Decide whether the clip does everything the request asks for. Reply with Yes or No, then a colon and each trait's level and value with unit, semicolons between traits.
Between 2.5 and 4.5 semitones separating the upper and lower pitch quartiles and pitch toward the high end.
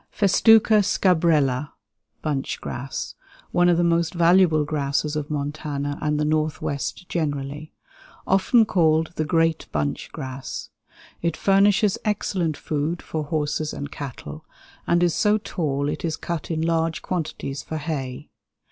No: average, 3.0 semitones; medium, 155 Hz